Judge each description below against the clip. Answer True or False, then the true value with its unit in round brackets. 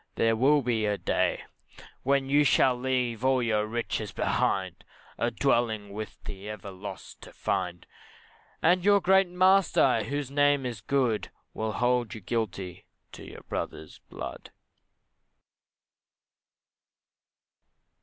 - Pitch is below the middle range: True (120 Hz)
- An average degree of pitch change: True (4.6 semitones)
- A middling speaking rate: False (125 wpm)